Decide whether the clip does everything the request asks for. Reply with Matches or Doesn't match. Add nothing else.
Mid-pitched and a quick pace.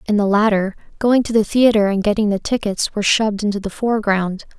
Doesn't match